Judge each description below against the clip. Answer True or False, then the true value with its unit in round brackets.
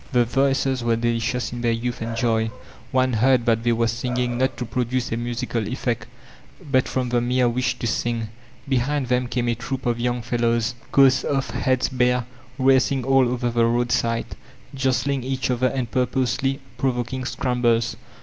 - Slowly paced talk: False (170 wpm)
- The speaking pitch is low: True (125 Hz)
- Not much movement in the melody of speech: True (1.7 semitones)